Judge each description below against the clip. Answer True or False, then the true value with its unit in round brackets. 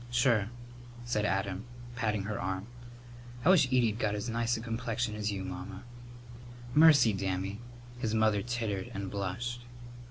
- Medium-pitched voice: False (110 Hz)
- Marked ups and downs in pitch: False (3.4 semitones)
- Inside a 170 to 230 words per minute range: False (145 wpm)